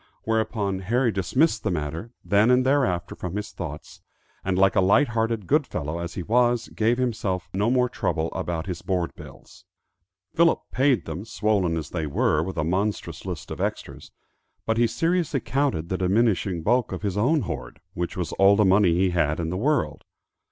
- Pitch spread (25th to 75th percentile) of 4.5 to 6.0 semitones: Yes, average, 5.3 semitones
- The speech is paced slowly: No, average, 185 wpm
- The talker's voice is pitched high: No, low, 100 Hz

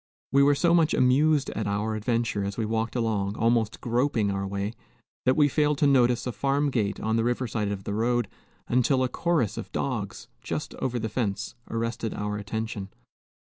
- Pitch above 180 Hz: No, low, 115 Hz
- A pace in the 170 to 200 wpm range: Yes, average, 190 wpm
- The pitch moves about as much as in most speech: Yes, average, 3.7 semitones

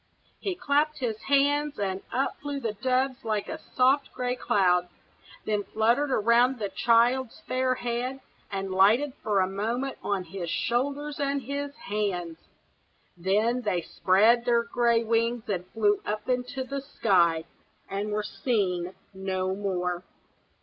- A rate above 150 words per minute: No, average, 145 wpm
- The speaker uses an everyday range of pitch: Yes, average, 4.9 semitones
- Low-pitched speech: No, high, 230 Hz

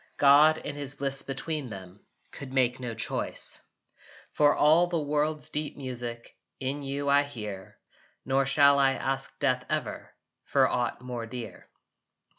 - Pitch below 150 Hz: Yes, low, 135 Hz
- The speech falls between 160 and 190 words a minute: No, average, 145 wpm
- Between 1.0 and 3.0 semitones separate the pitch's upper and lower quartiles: Yes, average, 2.7 semitones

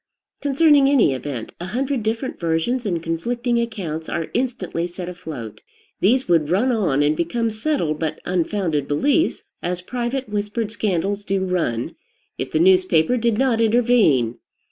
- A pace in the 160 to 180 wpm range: No, average, 145 wpm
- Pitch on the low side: No, high, 195 Hz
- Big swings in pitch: Yes, wide, 6.6 semitones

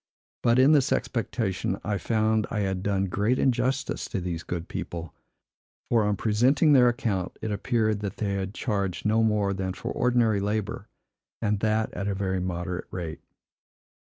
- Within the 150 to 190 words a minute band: Yes, average, 160 wpm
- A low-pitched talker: Yes, low, 105 Hz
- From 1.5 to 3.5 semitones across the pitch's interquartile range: Yes, average, 3.2 semitones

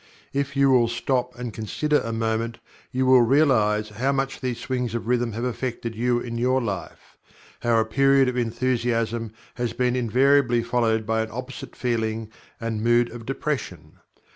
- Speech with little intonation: Yes, narrow, 2.2 semitones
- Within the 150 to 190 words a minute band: Yes, average, 165 wpm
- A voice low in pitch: Yes, low, 120 Hz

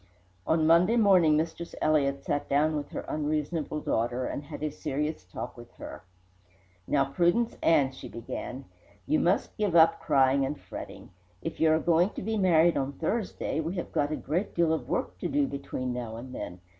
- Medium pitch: Yes, medium, 155 Hz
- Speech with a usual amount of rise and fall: Yes, average, 3.7 semitones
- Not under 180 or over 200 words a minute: Yes, average, 190 wpm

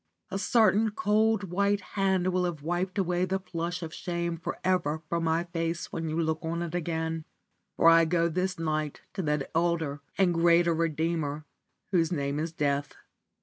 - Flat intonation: Yes, narrow, 2.2 semitones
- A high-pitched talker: No, medium, 170 Hz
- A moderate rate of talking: Yes, average, 175 wpm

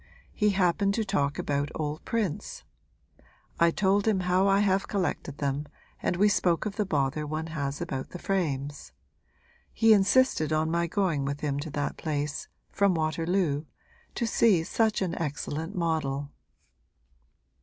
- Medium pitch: Yes, medium, 165 Hz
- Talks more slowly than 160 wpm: Yes, average, 150 wpm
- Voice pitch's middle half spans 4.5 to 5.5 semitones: Yes, average, 5.1 semitones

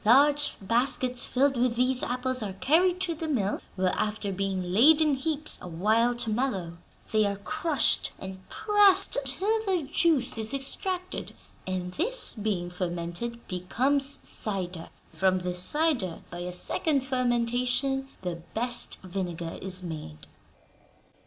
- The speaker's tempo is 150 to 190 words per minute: No, average, 140 wpm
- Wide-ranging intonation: Yes, wide, 7.1 semitones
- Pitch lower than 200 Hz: No, high, 240 Hz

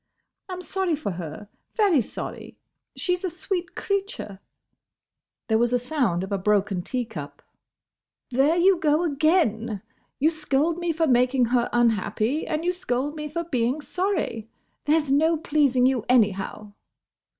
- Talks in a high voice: Yes, very high, 275 Hz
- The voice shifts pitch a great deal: Yes, wide, 6.6 semitones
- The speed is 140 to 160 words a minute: Yes, average, 150 wpm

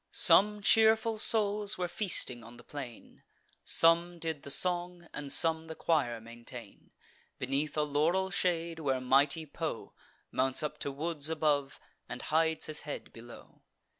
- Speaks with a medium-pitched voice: Yes, medium, 155 Hz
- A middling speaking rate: Yes, average, 145 wpm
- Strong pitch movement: No, average, 4.2 semitones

